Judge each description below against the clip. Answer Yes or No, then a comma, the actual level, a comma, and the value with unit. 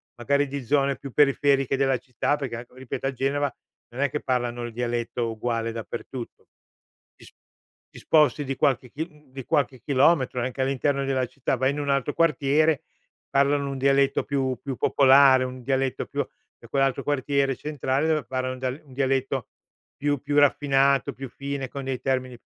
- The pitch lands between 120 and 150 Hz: Yes, low, 135 Hz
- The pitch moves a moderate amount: No, narrow, 1.7 semitones